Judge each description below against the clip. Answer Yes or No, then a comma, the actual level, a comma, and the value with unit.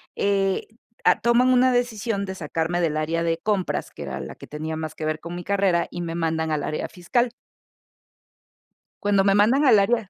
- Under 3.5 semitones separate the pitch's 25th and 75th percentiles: No, average, 5.0 semitones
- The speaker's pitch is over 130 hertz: Yes, high, 190 Hz